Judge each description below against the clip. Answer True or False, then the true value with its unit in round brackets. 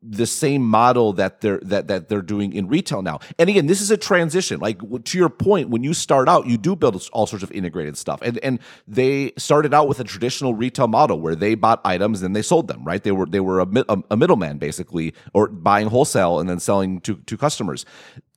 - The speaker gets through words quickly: True (230 wpm)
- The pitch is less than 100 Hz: False (115 Hz)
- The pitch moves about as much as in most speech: False (6.1 semitones)